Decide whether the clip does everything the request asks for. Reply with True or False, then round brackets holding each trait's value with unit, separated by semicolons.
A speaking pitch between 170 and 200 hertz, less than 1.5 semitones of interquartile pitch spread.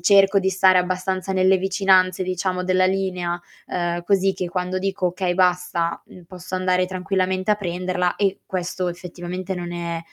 True (185 Hz; 1.0 semitones)